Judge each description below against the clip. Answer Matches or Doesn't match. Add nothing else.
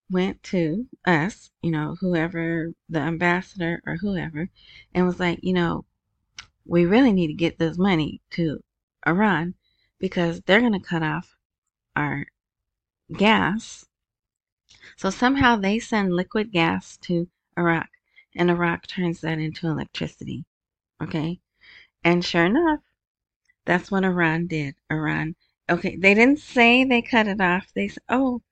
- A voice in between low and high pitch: Matches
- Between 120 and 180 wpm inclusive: Matches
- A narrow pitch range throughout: Doesn't match